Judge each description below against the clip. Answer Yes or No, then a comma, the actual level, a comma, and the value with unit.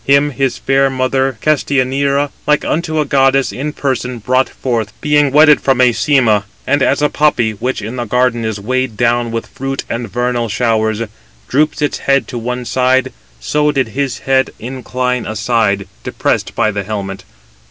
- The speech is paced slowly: No, average, 165 wpm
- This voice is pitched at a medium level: No, low, 130 Hz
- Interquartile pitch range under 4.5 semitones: Yes, average, 3.0 semitones